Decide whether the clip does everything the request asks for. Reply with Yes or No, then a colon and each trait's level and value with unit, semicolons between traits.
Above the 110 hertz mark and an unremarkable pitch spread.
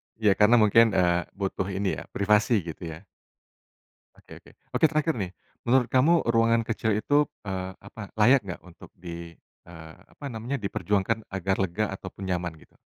No: low, 100 Hz; average, 3.9 semitones